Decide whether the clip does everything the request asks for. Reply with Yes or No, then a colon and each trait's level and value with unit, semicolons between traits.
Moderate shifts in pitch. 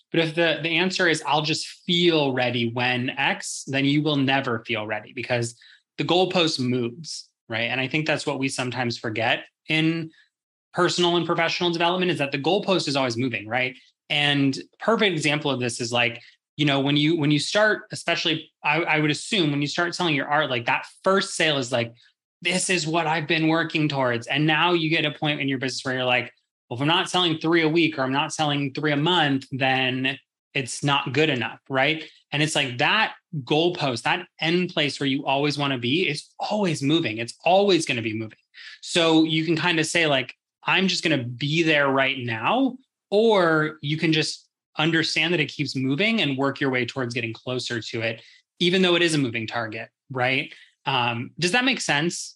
Yes: average, 4.3 semitones